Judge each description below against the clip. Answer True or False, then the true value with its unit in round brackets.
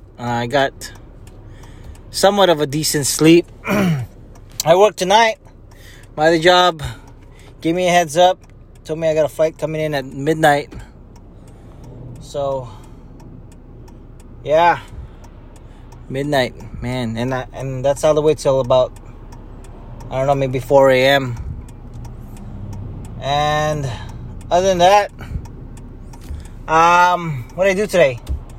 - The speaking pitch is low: True (130 Hz)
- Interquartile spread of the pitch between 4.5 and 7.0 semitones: True (5.1 semitones)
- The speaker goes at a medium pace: False (120 wpm)